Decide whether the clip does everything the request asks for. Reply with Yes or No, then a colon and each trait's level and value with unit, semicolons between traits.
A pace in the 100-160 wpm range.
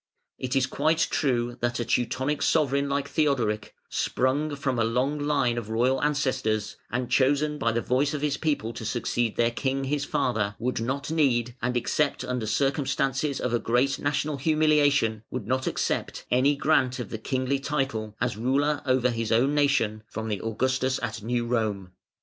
No: average, 175 wpm